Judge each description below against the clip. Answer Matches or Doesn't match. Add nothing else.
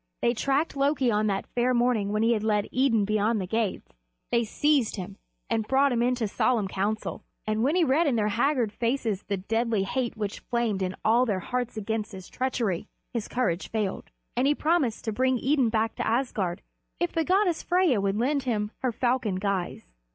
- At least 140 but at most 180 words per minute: Doesn't match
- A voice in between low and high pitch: Doesn't match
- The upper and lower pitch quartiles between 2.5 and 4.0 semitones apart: Matches